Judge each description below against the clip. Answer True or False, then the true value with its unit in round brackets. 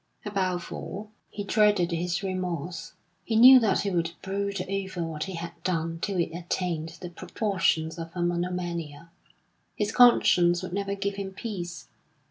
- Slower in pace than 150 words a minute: False (155 wpm)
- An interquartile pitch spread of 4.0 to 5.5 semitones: False (2.7 semitones)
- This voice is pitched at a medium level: True (180 Hz)